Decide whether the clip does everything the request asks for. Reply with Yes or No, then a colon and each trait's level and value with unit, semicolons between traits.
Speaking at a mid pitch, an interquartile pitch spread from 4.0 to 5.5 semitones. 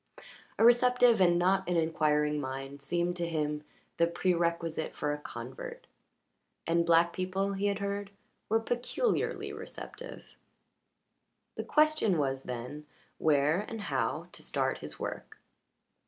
Yes: medium, 170 Hz; average, 5.1 semitones